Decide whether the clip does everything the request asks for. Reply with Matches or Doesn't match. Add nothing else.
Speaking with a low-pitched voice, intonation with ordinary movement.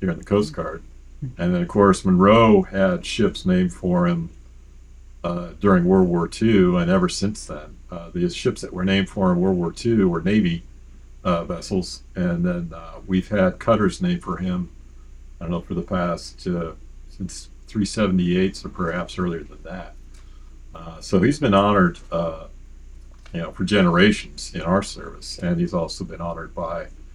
Doesn't match